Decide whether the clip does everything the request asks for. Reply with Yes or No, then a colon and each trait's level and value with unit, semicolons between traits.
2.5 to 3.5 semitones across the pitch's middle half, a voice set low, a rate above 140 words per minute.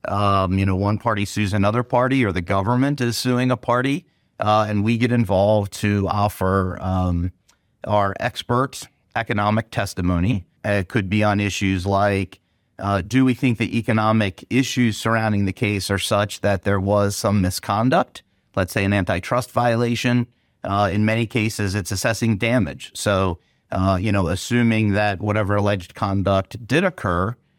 Yes: average, 3.2 semitones; low, 105 Hz; average, 160 wpm